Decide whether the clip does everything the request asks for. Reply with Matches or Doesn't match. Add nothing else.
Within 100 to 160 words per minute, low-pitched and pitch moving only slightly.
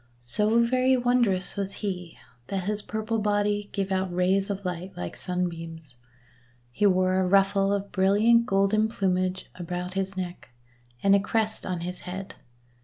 Doesn't match